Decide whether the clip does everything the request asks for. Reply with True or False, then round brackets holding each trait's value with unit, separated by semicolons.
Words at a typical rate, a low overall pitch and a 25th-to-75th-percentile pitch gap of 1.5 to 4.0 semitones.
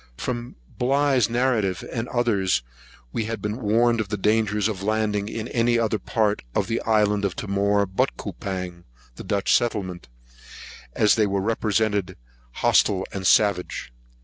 True (150 wpm; 105 Hz; 2.6 semitones)